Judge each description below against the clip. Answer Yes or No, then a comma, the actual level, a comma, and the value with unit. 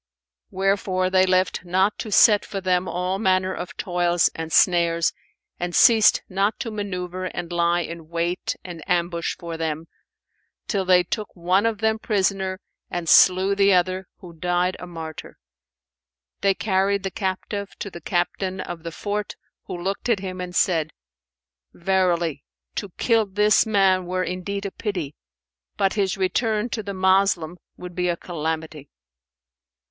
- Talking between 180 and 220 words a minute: No, average, 155 wpm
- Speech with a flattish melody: Yes, narrow, 2.2 semitones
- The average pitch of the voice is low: No, medium, 185 Hz